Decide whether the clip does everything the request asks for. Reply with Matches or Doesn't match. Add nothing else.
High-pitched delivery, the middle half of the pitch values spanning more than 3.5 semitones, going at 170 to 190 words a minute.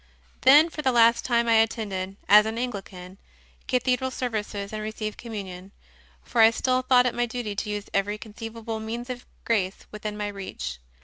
Doesn't match